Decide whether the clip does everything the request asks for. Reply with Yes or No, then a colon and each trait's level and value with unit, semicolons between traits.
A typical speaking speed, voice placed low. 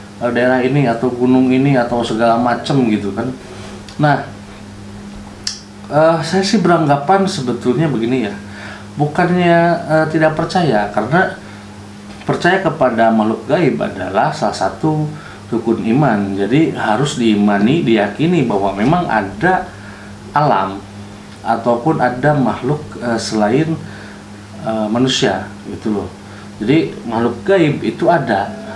Yes: average, 115 wpm; low, 115 Hz